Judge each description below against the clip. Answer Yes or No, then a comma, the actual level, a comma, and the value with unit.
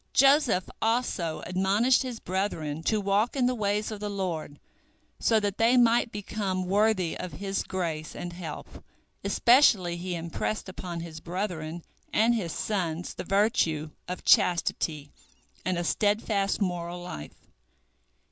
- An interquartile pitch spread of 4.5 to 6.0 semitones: No, average, 3.9 semitones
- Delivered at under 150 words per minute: Yes, average, 140 wpm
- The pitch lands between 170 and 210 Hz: Yes, high, 190 Hz